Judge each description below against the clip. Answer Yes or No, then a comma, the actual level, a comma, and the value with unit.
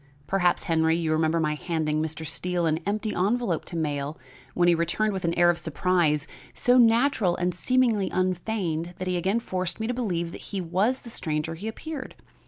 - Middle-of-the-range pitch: Yes, medium, 175 Hz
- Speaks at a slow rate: No, average, 190 wpm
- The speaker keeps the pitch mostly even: No, average, 4.6 semitones